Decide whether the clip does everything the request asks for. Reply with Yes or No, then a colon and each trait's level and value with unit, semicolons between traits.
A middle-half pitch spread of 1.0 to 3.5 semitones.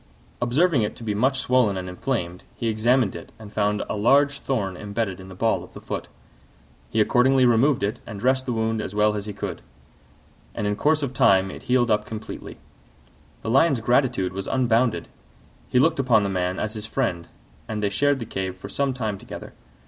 No: average, 4.1 semitones